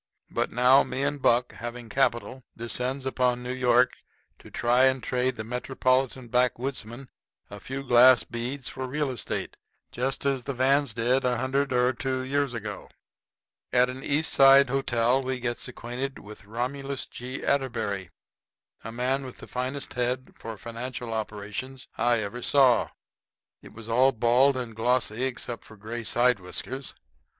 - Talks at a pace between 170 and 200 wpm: No, average, 155 wpm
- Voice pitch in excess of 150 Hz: No, low, 125 Hz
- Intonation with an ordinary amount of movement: No, narrow, 2.0 semitones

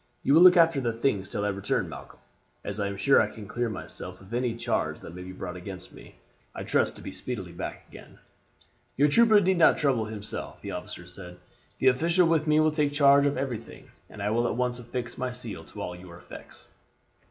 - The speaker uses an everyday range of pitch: No, wide, 6.3 semitones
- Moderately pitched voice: No, low, 120 Hz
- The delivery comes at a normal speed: No, fast, 220 wpm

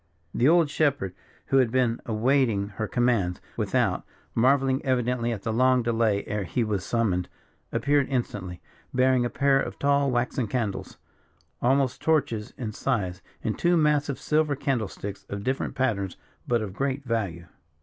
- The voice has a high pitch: No, low, 120 Hz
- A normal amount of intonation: Yes, average, 4.2 semitones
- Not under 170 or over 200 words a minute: No, average, 155 wpm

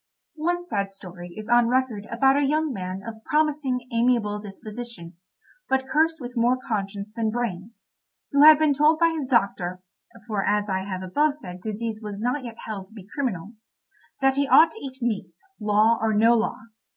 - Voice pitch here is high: Yes, high, 230 Hz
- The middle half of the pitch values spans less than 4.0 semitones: No, average, 4.8 semitones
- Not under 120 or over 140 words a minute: No, average, 185 wpm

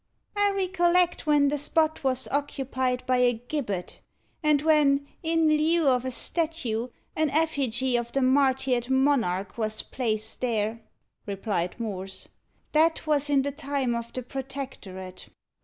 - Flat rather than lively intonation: No, average, 4.4 semitones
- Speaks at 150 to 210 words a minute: No, average, 140 wpm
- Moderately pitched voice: No, very high, 265 Hz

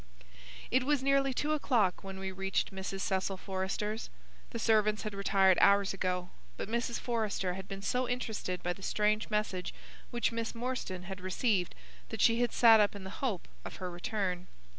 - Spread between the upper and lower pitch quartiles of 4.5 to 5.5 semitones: No, average, 3.5 semitones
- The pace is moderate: Yes, average, 180 wpm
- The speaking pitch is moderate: No, high, 200 Hz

